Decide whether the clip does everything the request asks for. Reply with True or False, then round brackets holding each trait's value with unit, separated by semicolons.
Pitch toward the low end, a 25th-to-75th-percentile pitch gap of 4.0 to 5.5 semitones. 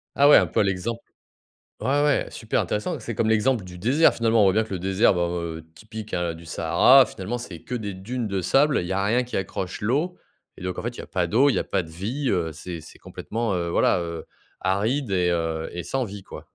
True (100 Hz; 5.0 semitones)